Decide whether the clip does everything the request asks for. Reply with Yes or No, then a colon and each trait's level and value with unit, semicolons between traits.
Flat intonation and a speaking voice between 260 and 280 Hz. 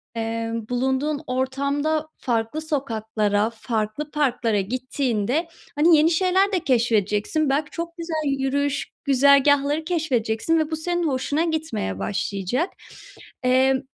No: wide, 5.4 semitones; very high, 275 Hz